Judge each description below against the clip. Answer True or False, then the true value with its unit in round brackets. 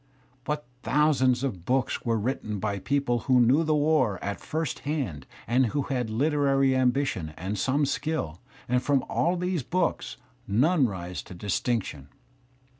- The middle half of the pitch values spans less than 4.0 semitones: False (5.5 semitones)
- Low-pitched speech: True (130 Hz)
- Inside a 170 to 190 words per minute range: False (150 wpm)